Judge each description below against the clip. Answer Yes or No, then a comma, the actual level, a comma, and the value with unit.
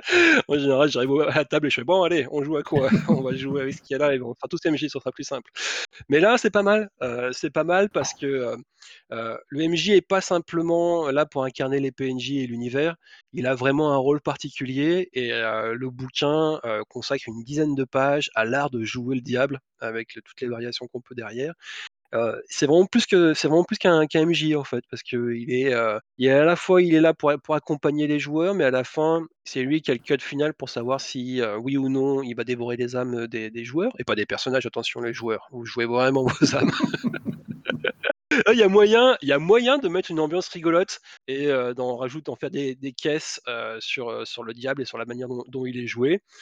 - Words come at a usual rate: No, fast, 245 wpm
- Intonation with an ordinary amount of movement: Yes, average, 4.0 semitones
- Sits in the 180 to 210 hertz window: No, medium, 140 Hz